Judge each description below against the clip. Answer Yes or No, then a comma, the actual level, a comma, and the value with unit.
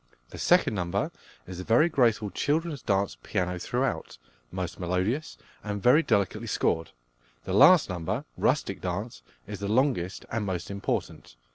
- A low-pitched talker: Yes, low, 100 Hz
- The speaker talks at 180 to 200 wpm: No, average, 145 wpm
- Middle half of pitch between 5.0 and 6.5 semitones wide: Yes, average, 5.3 semitones